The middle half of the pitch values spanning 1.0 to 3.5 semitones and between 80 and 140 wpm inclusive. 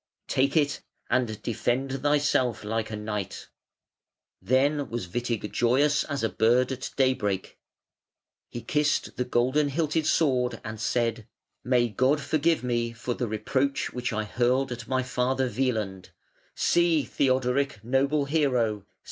Yes: average, 3.2 semitones; slow, 135 wpm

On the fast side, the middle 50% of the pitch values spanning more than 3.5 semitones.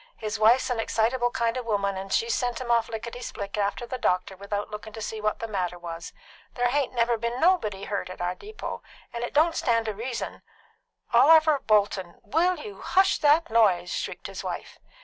Yes: fast, 210 wpm; average, 3.9 semitones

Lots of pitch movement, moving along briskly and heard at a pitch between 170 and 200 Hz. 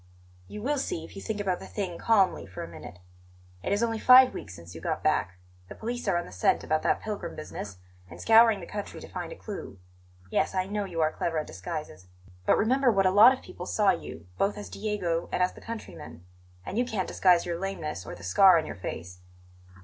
Yes: wide, 5.7 semitones; fast, 230 wpm; medium, 185 Hz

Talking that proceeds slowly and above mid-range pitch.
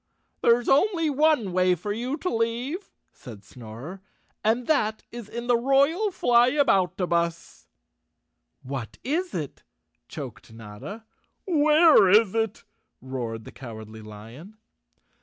Yes: slow, 120 wpm; high, 220 Hz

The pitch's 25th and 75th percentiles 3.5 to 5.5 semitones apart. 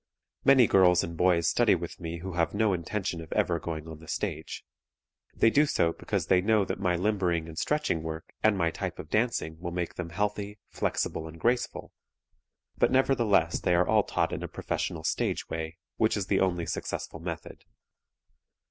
Yes: average, 4.0 semitones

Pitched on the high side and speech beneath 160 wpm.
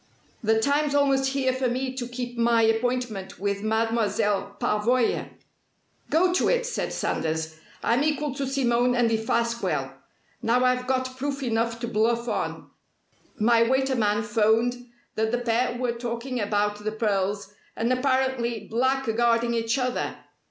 Yes: high, 235 Hz; average, 145 wpm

